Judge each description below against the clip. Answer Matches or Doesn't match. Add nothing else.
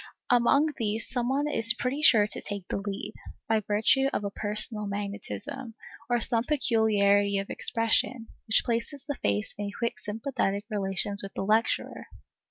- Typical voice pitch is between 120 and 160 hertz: Doesn't match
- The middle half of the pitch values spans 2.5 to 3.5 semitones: Matches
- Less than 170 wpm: Matches